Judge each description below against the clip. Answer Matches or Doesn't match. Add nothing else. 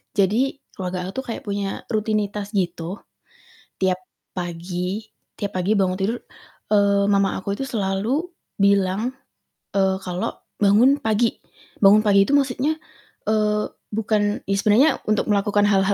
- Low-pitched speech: Doesn't match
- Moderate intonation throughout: Doesn't match